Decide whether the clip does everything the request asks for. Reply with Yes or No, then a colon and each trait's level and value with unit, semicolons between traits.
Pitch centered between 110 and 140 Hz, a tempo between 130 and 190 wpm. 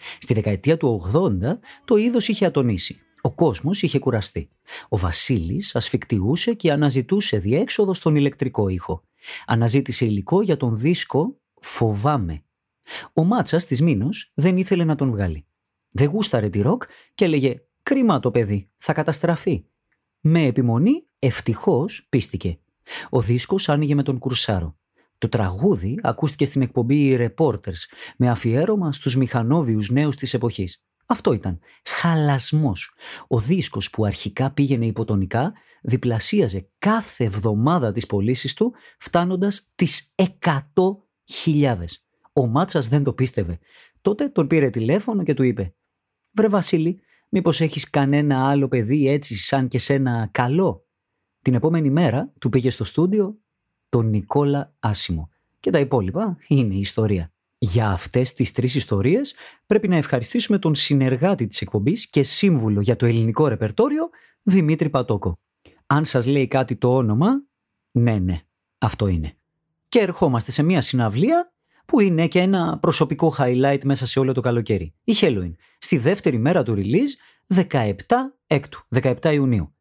Yes: low, 135 Hz; average, 140 wpm